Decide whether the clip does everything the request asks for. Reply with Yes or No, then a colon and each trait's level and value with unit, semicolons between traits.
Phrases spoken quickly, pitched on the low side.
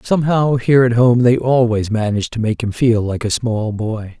Yes: fast, 215 wpm; low, 115 Hz